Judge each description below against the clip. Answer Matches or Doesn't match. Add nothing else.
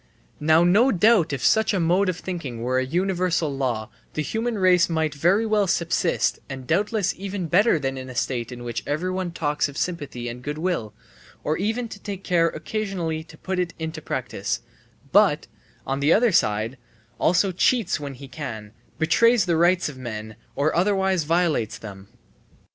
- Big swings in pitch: Matches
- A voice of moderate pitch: Matches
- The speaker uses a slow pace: Doesn't match